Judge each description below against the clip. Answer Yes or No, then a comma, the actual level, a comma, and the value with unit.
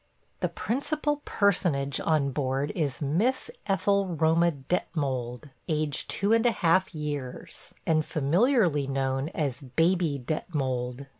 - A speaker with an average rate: No, slow, 120 wpm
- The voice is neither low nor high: Yes, medium, 155 Hz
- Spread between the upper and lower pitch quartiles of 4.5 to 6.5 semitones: Yes, average, 5.1 semitones